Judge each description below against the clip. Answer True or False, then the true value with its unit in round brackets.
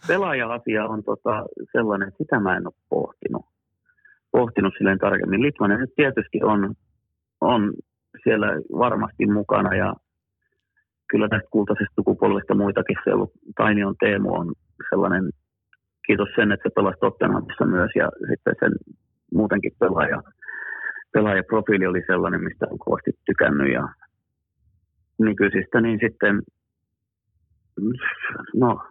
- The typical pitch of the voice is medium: False (100 Hz)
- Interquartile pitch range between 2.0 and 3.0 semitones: True (2.7 semitones)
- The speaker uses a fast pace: False (115 wpm)